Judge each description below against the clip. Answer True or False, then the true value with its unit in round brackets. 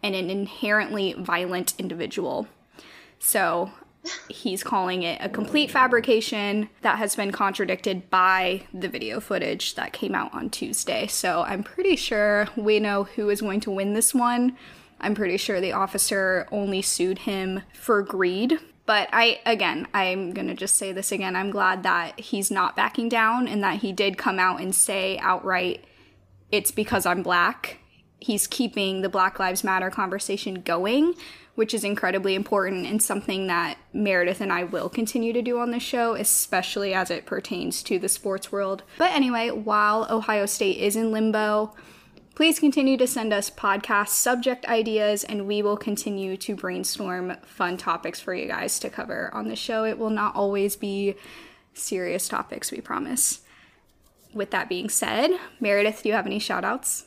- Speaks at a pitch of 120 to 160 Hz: False (205 Hz)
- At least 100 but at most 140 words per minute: False (170 wpm)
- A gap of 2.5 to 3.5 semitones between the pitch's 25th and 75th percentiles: True (2.9 semitones)